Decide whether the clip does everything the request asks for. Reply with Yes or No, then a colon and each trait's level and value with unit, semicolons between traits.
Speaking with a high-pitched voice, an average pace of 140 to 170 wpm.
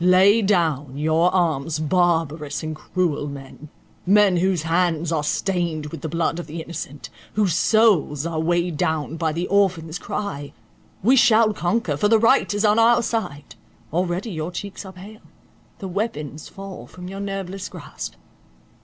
No: medium, 175 Hz; average, 155 wpm